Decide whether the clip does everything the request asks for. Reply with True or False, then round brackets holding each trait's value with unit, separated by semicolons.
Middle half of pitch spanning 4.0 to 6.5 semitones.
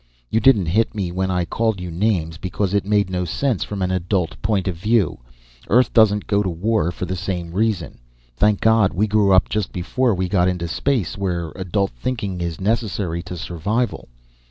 False (3.3 semitones)